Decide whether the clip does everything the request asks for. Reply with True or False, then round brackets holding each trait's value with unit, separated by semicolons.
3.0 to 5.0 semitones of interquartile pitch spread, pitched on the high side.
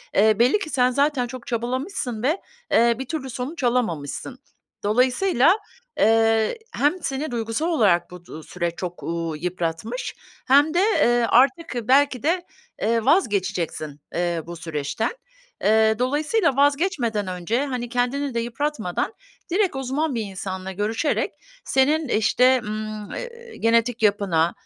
False (5.5 semitones; 240 Hz)